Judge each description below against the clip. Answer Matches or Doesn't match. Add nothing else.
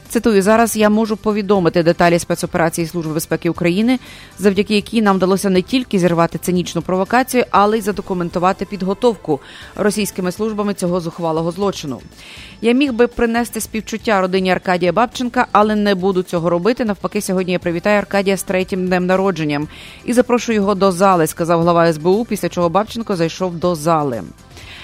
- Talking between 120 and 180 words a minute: Matches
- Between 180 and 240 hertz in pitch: Matches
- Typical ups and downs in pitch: Matches